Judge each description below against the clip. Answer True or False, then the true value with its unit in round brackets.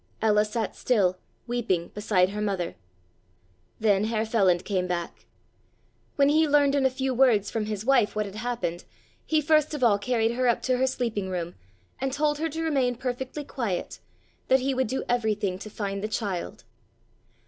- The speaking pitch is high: True (225 Hz)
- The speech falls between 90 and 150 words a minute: False (180 wpm)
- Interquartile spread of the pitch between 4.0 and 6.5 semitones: True (4.6 semitones)